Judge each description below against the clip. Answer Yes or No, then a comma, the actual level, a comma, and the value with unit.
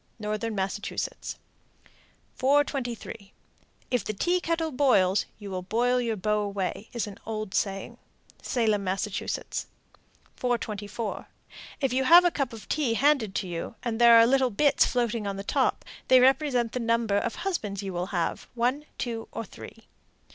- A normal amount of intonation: Yes, average, 4.0 semitones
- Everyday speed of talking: Yes, average, 155 wpm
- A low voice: No, high, 230 Hz